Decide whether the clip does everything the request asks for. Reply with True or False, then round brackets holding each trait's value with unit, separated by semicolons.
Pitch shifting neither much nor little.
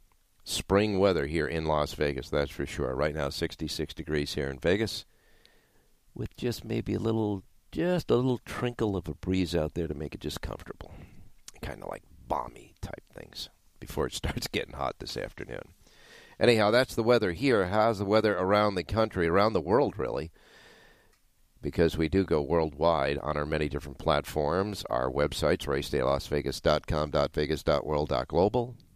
False (5.9 semitones)